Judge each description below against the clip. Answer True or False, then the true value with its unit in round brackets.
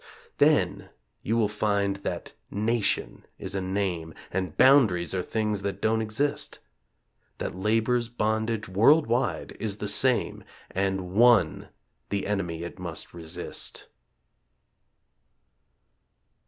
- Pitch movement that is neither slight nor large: True (3.2 semitones)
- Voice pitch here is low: True (100 Hz)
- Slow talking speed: True (110 wpm)